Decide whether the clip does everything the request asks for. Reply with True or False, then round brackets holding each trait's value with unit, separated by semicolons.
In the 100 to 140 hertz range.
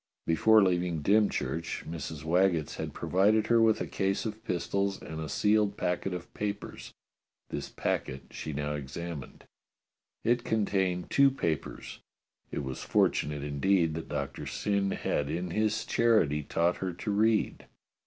False (90 Hz)